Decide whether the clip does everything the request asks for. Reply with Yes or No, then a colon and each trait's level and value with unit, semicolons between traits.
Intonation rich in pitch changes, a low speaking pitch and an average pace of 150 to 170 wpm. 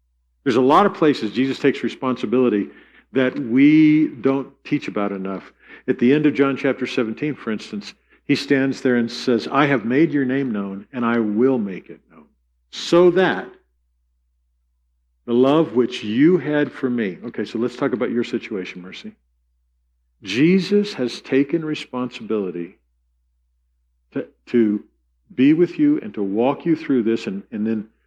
Yes: wide, 7.6 semitones; low, 120 Hz; average, 160 wpm